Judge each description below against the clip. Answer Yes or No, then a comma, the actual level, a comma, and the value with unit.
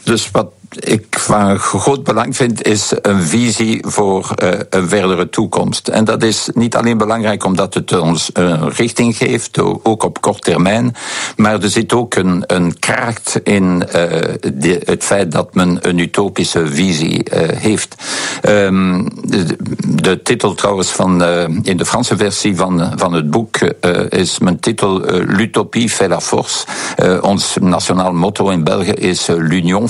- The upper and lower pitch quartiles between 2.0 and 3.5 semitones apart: No, average, 4.0 semitones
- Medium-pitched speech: No, low, 100 Hz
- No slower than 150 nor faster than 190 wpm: No, average, 140 wpm